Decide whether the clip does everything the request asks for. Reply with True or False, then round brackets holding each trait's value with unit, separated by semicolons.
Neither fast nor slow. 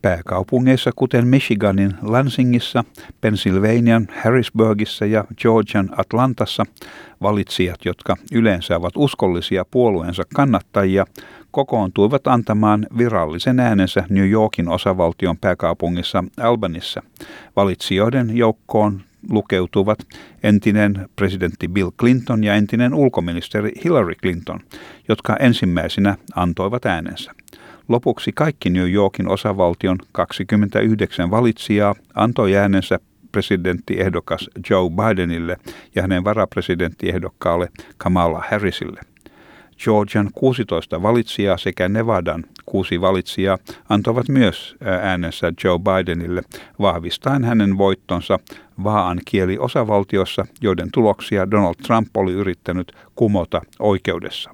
False (90 wpm)